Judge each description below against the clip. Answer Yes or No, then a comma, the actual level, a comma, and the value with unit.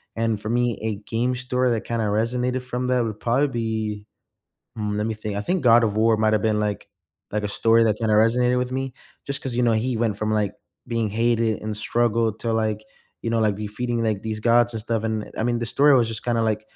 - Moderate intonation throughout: No, narrow, 1.9 semitones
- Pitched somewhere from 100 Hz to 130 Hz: Yes, low, 115 Hz